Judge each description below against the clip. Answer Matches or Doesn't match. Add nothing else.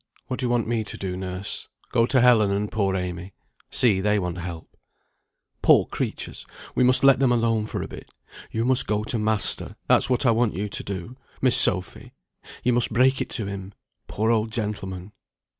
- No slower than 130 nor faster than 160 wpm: Doesn't match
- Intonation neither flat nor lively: Matches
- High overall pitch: Doesn't match